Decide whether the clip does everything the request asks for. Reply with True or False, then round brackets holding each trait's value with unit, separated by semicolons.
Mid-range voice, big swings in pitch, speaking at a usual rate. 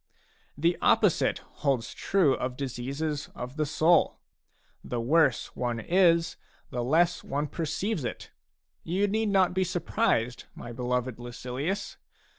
False (150 Hz; 5.7 semitones; 125 wpm)